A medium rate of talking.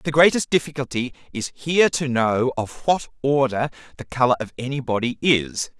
Yes: average, 165 wpm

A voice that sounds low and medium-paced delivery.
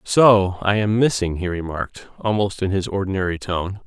Yes: very low, 95 Hz; average, 170 wpm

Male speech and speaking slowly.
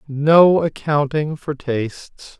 Yes: male; slow, 100 wpm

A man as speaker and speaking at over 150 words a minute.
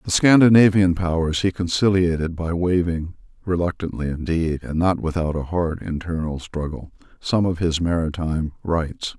No: male; slow, 135 wpm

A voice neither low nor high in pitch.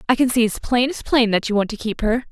No: high, 230 Hz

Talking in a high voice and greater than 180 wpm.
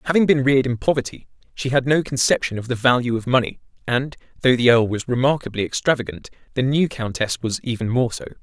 No: low, 125 Hz; average, 200 wpm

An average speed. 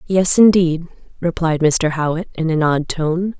Yes: average, 160 wpm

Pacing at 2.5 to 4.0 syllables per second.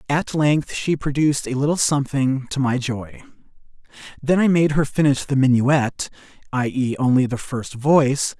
No: 4.8 syllables/s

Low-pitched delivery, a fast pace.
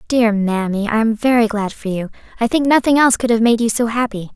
No: high, 225 Hz; fast, 250 wpm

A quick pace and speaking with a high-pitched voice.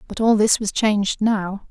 Yes: fast, 210 wpm; high, 210 Hz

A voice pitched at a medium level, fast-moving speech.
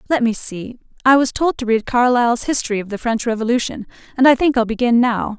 No: high, 240 Hz; fast, 225 wpm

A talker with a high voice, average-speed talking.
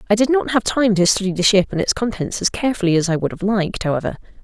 No: high, 200 Hz; fast, 270 wpm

